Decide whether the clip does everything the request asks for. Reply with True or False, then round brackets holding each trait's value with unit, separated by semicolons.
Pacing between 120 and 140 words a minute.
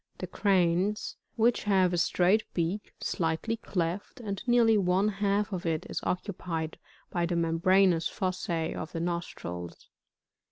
True (135 wpm)